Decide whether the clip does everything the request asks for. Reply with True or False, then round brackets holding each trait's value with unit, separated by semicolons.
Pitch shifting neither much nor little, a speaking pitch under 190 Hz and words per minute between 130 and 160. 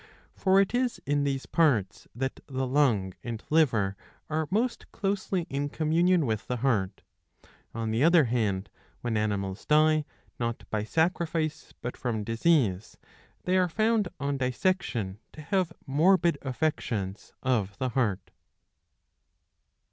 False (6.9 semitones; 135 Hz; 135 wpm)